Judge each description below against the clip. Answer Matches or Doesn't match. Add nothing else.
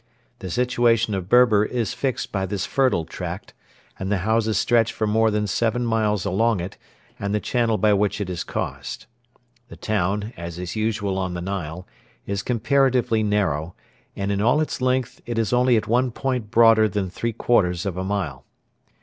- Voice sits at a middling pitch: Doesn't match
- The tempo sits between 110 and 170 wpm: Doesn't match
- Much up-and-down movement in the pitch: Doesn't match